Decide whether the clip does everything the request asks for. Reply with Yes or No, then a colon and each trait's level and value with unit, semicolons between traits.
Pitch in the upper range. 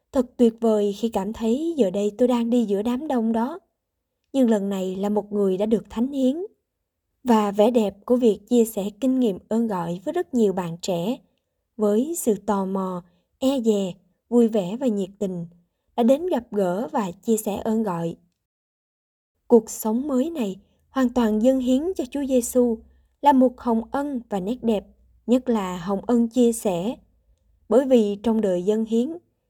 Yes: high, 225 Hz